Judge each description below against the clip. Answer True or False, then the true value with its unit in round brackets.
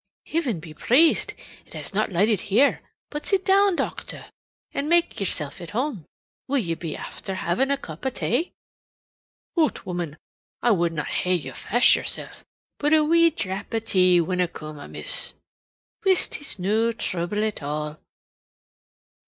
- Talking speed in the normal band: True (155 wpm)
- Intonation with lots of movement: True (8.8 semitones)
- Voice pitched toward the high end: True (210 Hz)